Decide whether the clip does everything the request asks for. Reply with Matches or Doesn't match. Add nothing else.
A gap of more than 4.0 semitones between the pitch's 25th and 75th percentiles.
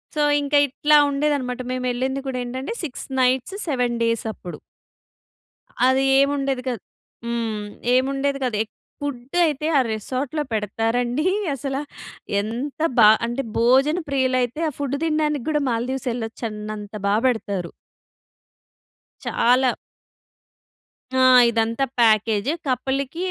Doesn't match